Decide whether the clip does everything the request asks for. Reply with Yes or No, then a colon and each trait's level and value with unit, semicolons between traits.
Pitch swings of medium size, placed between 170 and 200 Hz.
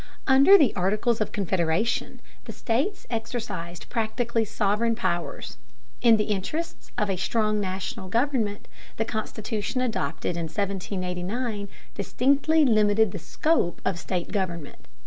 No: average, 4.0 semitones; high, 215 Hz